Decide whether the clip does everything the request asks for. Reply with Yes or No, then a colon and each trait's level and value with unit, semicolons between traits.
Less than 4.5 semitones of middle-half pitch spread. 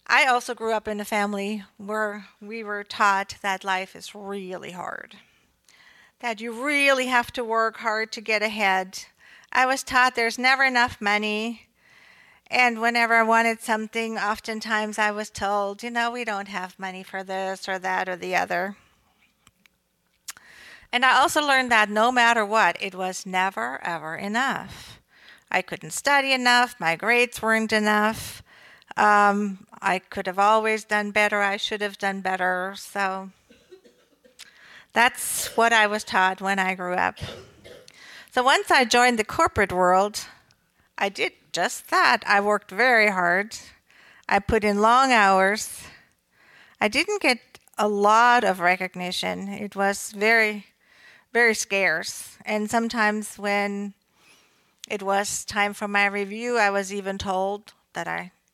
Yes: average, 2.8 semitones